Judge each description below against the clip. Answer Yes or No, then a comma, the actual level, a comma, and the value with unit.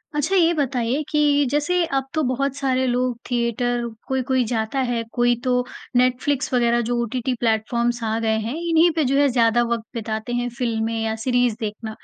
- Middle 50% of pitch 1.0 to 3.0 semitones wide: Yes, narrow, 2.5 semitones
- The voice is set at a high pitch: Yes, high, 245 Hz